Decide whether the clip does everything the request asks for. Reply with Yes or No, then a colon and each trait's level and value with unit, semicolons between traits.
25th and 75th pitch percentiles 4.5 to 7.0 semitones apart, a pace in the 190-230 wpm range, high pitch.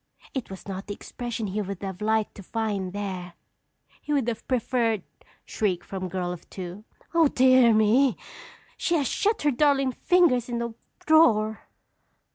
No: average, 4.8 semitones; average, 165 wpm; high, 220 Hz